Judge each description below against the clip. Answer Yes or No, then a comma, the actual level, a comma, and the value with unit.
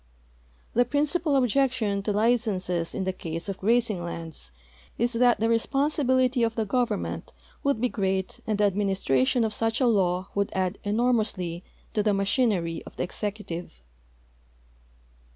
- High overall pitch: Yes, high, 210 Hz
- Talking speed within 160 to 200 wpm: No, average, 150 wpm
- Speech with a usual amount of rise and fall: Yes, average, 4.4 semitones